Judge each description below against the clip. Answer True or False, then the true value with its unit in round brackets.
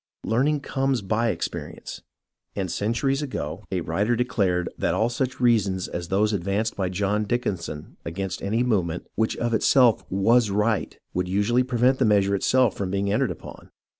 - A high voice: False (105 Hz)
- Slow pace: False (165 wpm)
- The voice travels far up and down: False (3.9 semitones)